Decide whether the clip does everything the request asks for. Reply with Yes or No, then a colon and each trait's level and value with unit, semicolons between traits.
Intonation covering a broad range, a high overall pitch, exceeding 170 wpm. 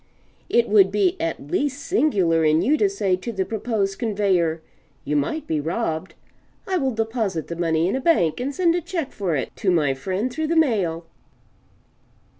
Yes: wide, 8.0 semitones; high, 200 Hz; average, 185 wpm